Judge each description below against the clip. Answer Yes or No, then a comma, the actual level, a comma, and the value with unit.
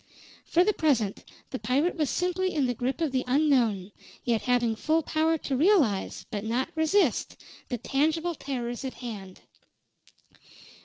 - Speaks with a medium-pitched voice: No, very high, 270 Hz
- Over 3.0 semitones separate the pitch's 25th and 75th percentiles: Yes, average, 5.1 semitones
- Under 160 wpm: Yes, average, 150 wpm